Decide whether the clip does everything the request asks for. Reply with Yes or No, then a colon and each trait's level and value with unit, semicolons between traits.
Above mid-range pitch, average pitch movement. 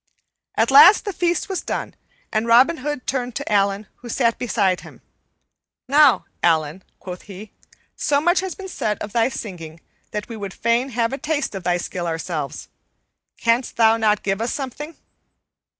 No: high, 230 Hz; wide, 5.9 semitones